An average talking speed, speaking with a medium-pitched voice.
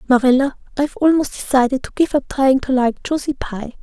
No: average, 190 wpm; very high, 270 Hz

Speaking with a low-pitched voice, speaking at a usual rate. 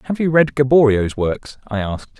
Yes: low, 125 Hz; average, 190 wpm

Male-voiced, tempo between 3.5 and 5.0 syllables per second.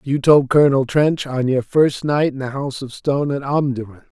No: male; 5.4 syllables/s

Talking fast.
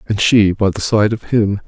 Yes: fast, 250 wpm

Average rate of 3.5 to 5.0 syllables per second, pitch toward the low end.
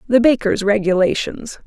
No: 4.7 syllables/s; high, 220 Hz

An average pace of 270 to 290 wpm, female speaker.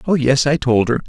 No: fast, 280 wpm; male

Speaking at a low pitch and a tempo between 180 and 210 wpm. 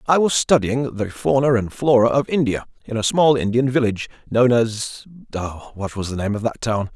Yes: low, 120 Hz; average, 200 wpm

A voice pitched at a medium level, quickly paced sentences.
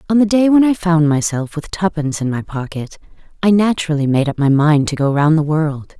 Yes: medium, 160 Hz; fast, 230 wpm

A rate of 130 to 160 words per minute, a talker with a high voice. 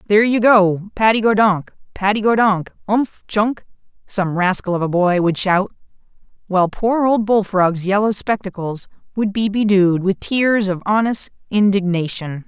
Yes: average, 150 wpm; high, 200 Hz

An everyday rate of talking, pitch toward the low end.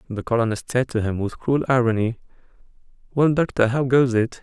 Yes: average, 175 wpm; low, 120 Hz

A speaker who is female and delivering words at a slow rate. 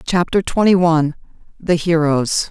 Yes: female; slow, 95 wpm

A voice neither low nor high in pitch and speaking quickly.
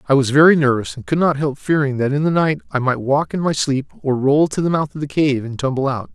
Yes: medium, 145 Hz; fast, 295 wpm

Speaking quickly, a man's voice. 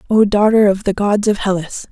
No: fast, 220 wpm; female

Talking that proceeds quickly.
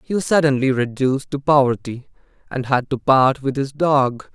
No: average, 180 wpm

